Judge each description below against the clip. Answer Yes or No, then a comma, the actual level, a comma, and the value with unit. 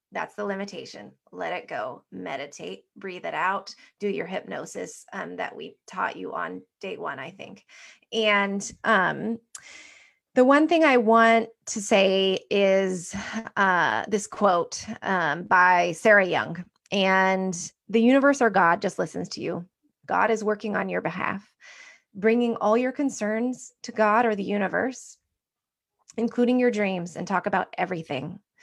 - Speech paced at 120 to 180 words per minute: Yes, average, 150 wpm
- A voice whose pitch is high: Yes, high, 210 Hz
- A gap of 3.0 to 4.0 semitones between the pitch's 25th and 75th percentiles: Yes, average, 3.6 semitones